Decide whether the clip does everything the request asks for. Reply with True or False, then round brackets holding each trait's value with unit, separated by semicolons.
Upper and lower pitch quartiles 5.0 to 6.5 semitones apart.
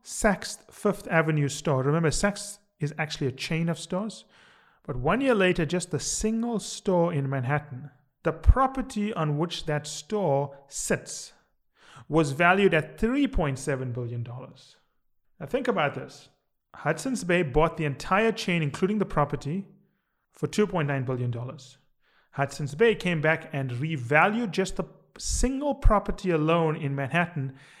True (5.5 semitones)